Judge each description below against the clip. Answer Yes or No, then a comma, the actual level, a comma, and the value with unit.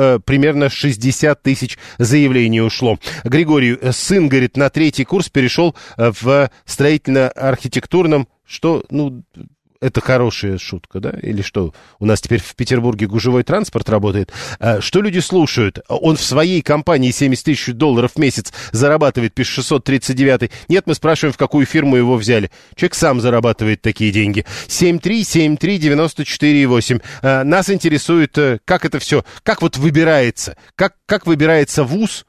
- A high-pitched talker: No, low, 135 Hz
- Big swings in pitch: No, average, 4.6 semitones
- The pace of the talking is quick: No, average, 130 wpm